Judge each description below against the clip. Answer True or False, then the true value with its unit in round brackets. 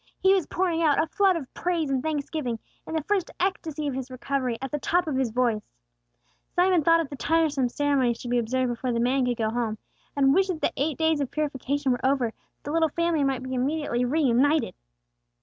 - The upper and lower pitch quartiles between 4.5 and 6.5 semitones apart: False (4.1 semitones)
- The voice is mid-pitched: False (280 Hz)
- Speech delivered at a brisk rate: True (220 wpm)